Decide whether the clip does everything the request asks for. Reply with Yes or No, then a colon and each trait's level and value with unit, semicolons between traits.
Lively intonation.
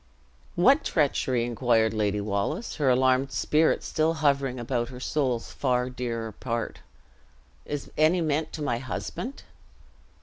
No: average, 4.3 semitones